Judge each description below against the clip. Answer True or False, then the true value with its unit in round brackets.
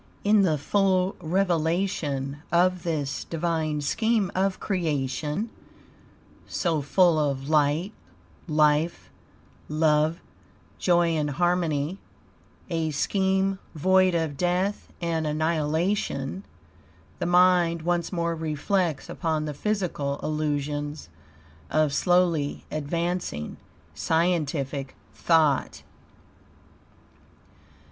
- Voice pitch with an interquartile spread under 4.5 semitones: True (3.3 semitones)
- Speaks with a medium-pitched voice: True (165 Hz)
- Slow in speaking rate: True (85 wpm)